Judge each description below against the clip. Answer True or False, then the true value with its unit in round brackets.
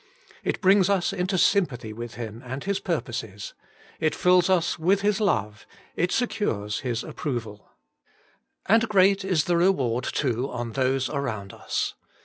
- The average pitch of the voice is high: False (150 Hz)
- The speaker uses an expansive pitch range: True (8.3 semitones)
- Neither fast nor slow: True (150 wpm)